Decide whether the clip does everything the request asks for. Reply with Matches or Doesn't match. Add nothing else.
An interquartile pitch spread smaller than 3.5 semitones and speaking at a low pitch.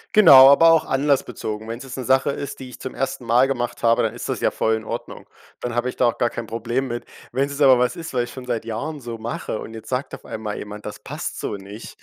Matches